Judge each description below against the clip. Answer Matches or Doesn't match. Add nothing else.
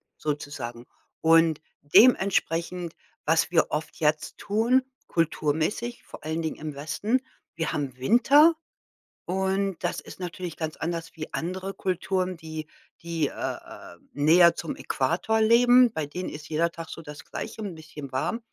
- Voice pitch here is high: Doesn't match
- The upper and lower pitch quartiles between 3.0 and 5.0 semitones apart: Matches